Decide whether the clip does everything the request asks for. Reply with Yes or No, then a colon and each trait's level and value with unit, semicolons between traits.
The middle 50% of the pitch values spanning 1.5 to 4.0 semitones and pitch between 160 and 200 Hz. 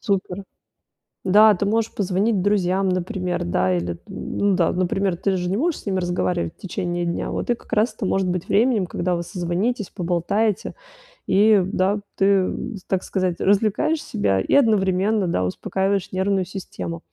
Yes: narrow, 2.6 semitones; high, 190 Hz